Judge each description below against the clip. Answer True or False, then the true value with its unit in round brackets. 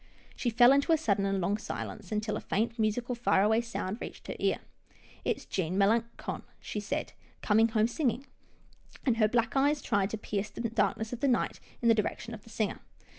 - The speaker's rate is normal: False (210 wpm)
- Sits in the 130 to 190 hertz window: False (225 Hz)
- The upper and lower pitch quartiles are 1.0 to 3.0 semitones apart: True (2.4 semitones)